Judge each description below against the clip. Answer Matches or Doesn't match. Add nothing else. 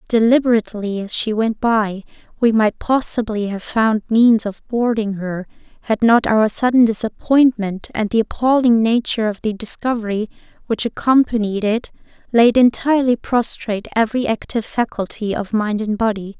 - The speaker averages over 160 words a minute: Doesn't match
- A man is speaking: Doesn't match